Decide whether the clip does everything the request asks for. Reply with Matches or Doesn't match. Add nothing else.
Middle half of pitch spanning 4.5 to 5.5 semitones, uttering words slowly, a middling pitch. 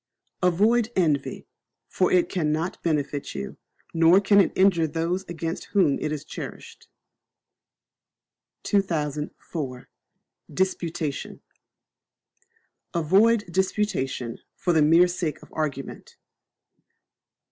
Doesn't match